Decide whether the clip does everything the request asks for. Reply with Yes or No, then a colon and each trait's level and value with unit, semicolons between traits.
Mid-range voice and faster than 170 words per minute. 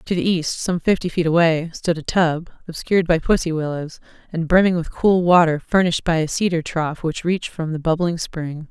Yes: medium, 165 Hz; fast, 205 wpm